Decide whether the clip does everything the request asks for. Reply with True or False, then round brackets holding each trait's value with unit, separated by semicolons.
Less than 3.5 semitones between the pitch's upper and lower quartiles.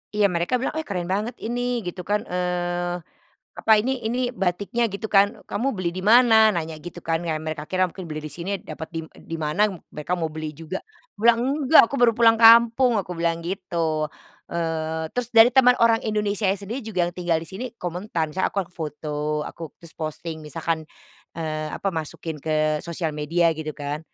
False (5.0 semitones)